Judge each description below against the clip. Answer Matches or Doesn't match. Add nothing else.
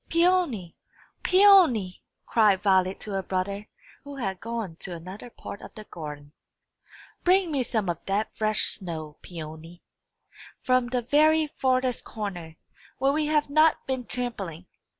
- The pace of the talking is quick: Doesn't match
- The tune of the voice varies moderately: Doesn't match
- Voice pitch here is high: Matches